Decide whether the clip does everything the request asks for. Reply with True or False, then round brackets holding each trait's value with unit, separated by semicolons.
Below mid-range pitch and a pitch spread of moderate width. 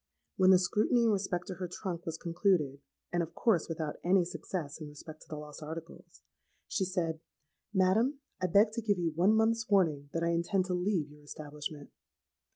False (175 Hz; 3.6 semitones)